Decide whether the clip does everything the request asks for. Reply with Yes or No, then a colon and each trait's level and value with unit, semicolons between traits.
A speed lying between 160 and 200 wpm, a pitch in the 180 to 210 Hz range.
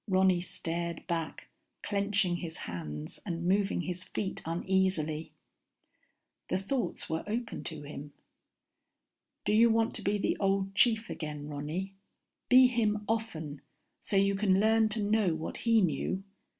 No: average, 140 wpm; high, 190 Hz